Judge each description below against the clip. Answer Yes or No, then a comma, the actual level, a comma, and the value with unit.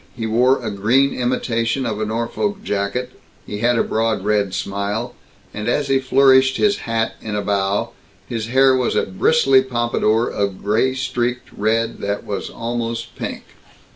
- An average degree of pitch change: Yes, average, 3.5 semitones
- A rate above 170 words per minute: No, average, 165 wpm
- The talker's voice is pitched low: Yes, low, 115 Hz